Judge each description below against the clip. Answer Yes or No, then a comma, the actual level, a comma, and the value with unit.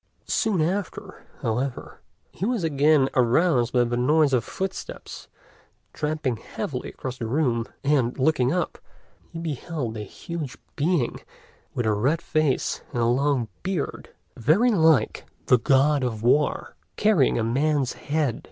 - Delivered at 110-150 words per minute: Yes, average, 140 wpm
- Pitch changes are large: No, average, 4.6 semitones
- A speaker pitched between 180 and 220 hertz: No, medium, 140 Hz